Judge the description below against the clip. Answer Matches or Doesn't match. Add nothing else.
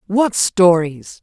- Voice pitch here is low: Doesn't match